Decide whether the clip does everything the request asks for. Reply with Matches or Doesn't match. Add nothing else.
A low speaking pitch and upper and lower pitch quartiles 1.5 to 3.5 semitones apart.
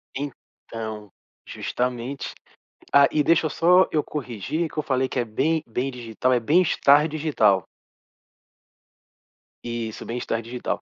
Doesn't match